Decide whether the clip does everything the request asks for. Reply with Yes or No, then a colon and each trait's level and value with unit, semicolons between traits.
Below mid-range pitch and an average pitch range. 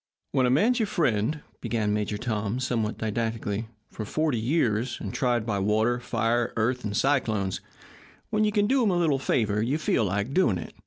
Yes: low, 115 Hz; average, 4.8 semitones